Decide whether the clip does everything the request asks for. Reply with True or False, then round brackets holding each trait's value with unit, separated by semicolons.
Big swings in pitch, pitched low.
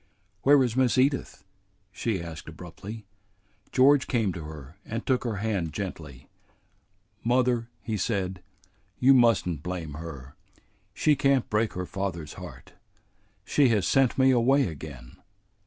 True (7.2 semitones; 105 Hz)